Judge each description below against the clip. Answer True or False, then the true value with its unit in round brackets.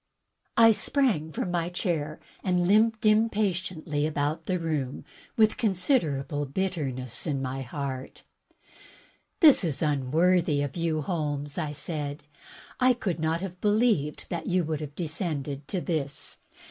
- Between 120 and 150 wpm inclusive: True (135 wpm)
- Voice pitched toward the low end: False (160 Hz)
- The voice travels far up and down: False (4.4 semitones)